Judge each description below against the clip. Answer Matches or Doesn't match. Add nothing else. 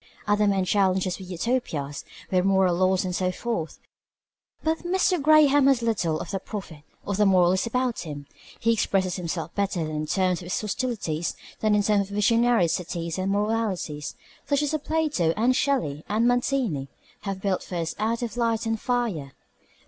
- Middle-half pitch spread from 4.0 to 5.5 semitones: Matches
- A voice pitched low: Doesn't match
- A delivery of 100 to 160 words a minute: Doesn't match